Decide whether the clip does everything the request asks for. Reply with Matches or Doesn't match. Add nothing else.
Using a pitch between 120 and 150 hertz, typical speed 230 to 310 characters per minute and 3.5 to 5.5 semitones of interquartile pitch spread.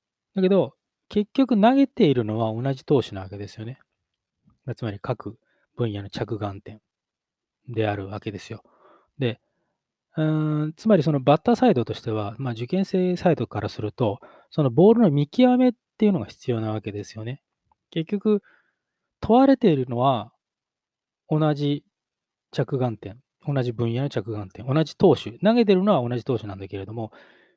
Doesn't match